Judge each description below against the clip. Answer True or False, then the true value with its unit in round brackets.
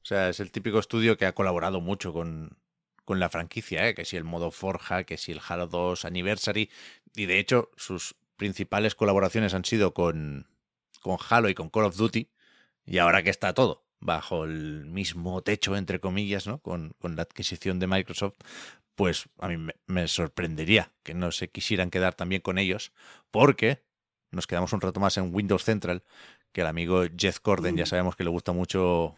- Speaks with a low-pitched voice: True (95 Hz)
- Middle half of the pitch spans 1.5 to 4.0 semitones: True (2.6 semitones)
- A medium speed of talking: False (195 wpm)